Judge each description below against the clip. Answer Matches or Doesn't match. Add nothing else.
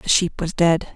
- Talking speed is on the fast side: Matches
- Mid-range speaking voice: Matches